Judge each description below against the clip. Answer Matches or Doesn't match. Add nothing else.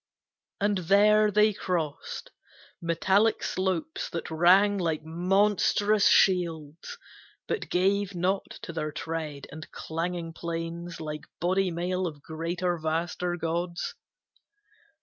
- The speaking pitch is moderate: Matches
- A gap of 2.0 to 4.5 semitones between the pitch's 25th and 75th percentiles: Matches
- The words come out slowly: Matches